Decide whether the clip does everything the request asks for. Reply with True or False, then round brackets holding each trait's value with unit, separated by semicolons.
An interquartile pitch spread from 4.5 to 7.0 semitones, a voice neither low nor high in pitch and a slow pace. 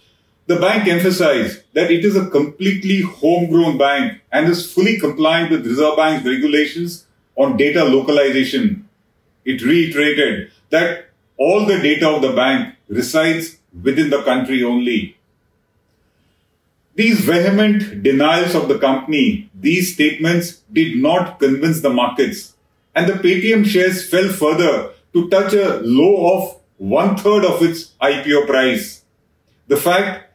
True (5.1 semitones; 165 Hz; 130 wpm)